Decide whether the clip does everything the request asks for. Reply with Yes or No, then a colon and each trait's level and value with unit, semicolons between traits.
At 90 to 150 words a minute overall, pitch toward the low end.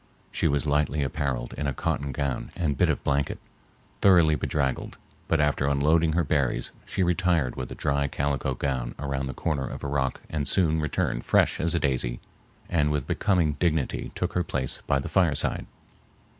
No: average, 180 wpm; very low, 70 Hz